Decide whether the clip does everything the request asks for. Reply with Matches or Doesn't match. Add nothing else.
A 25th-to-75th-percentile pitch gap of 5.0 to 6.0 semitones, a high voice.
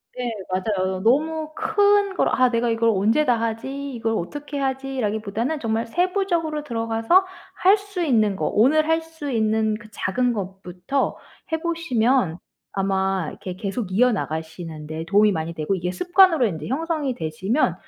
Doesn't match